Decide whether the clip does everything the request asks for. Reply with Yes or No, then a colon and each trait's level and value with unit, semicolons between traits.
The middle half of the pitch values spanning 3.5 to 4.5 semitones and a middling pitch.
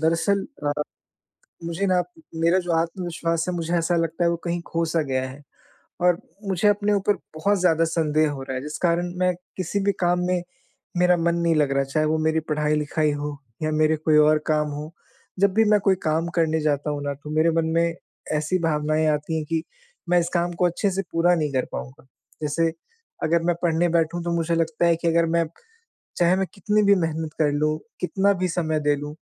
No: narrow, 2.4 semitones; medium, 165 Hz